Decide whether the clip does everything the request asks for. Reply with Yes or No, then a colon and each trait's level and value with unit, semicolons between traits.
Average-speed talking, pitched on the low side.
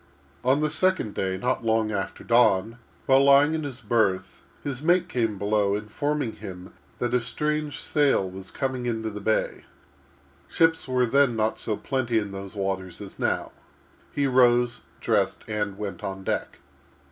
Yes: average, 160 wpm; low, 115 Hz